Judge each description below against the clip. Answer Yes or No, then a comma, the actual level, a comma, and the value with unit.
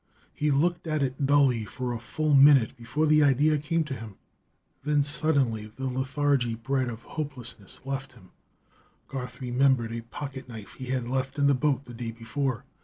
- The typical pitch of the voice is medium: No, low, 130 Hz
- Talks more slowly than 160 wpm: No, average, 180 wpm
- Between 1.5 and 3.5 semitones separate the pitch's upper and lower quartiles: Yes, average, 3.2 semitones